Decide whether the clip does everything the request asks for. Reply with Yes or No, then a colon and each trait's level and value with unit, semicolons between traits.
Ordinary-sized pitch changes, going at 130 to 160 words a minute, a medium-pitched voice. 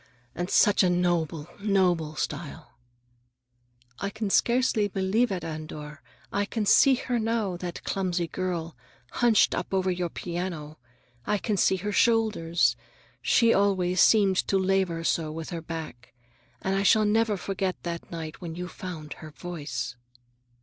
Yes: average, 3.6 semitones; average, 150 wpm; medium, 180 Hz